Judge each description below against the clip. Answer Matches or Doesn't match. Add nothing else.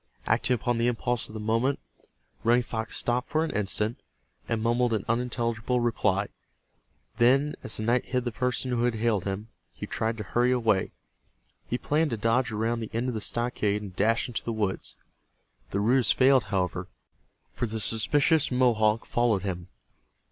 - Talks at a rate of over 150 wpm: Matches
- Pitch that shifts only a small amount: Matches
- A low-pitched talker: Matches